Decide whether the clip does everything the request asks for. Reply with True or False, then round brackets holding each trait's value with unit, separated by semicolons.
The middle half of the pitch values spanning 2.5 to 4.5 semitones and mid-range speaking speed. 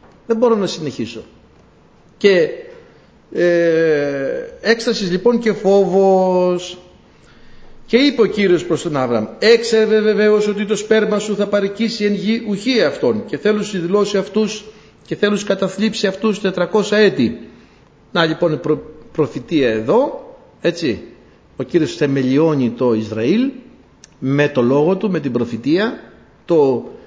False (5.0 semitones; 135 wpm)